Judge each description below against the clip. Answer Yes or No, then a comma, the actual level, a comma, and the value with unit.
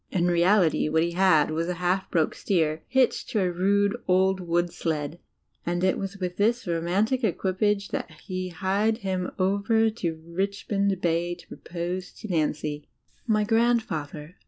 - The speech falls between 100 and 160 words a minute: Yes, average, 155 wpm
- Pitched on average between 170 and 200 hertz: Yes, medium, 185 Hz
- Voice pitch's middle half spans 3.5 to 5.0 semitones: No, average, 2.9 semitones